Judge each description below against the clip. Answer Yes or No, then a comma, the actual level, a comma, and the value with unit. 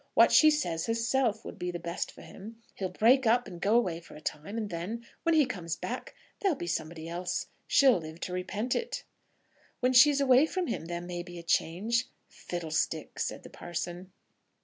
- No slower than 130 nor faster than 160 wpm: No, average, 195 wpm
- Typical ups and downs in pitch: No, wide, 6.1 semitones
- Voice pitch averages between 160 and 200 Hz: Yes, high, 190 Hz